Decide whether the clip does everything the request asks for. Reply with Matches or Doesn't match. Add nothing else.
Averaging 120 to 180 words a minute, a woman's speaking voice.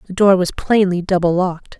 Doesn't match